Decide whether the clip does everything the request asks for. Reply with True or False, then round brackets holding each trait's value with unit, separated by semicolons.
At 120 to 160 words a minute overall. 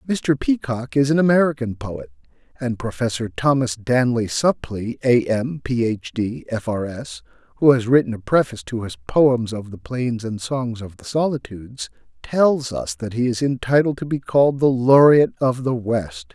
False (180 wpm)